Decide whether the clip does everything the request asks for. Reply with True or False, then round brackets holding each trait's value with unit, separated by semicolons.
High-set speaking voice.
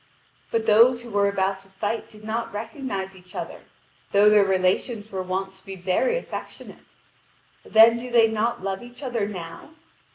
True (210 Hz)